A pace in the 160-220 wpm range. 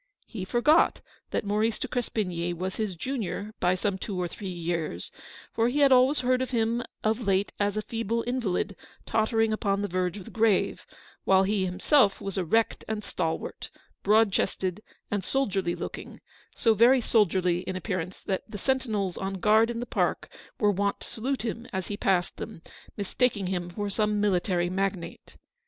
Yes: average, 180 wpm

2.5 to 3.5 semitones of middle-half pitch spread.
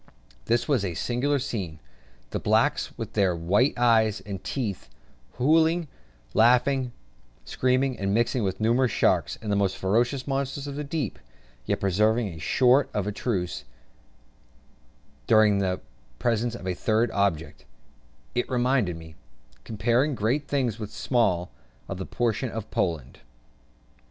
No: average, 4.7 semitones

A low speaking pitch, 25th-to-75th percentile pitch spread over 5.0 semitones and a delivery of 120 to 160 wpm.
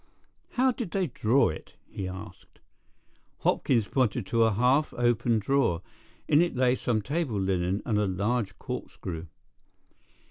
Yes: low, 115 Hz; wide, 5.5 semitones; average, 140 wpm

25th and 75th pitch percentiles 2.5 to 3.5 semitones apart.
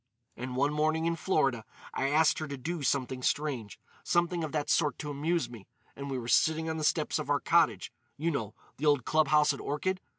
Yes: average, 2.9 semitones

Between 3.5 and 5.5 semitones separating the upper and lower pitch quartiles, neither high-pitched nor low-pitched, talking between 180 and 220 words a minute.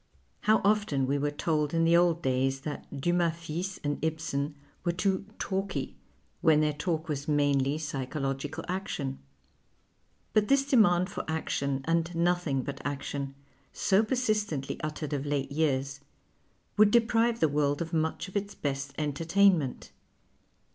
No: average, 4.5 semitones; medium, 160 Hz; average, 145 wpm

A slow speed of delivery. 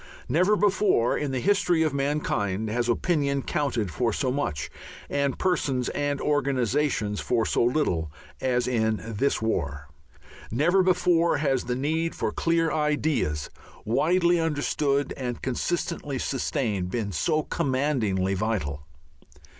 Yes: slow, 125 wpm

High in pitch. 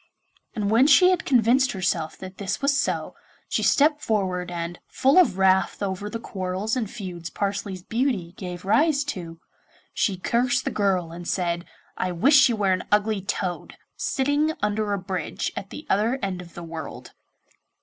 Yes: high, 200 Hz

